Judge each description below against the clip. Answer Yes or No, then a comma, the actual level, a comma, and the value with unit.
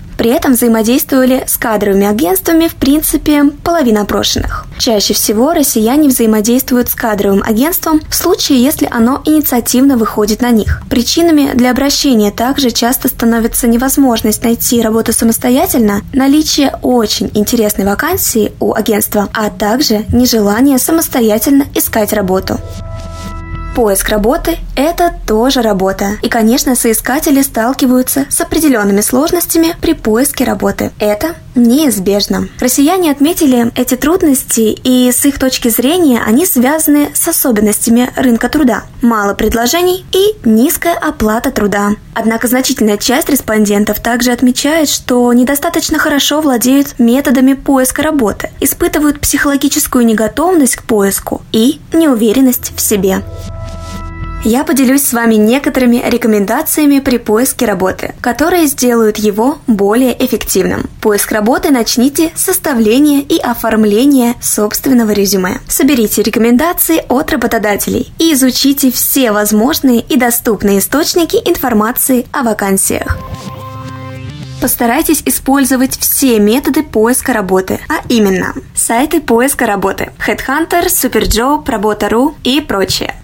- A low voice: No, high, 245 Hz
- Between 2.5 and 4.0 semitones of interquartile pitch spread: No, average, 4.7 semitones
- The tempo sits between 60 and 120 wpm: Yes, average, 115 wpm